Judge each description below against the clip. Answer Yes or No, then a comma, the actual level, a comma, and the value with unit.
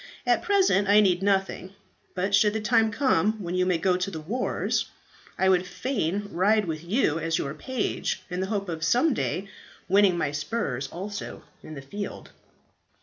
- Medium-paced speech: Yes, average, 180 wpm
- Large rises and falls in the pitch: No, average, 3.5 semitones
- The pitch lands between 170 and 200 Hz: Yes, high, 190 Hz